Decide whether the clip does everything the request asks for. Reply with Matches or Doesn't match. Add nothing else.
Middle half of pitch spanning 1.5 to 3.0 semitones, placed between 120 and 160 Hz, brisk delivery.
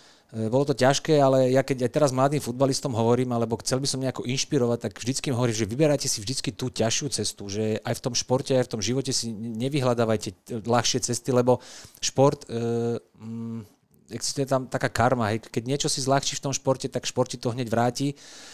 Matches